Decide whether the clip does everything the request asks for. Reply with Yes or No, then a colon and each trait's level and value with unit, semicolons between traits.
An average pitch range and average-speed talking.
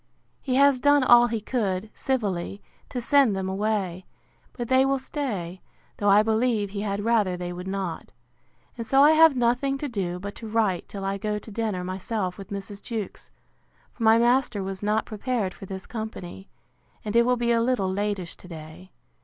Yes: average, 4.0 semitones; average, 190 wpm